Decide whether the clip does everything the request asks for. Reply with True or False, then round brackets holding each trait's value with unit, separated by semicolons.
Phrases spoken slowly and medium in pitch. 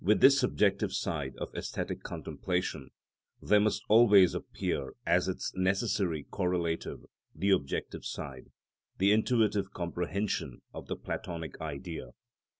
False (120 wpm; 95 Hz)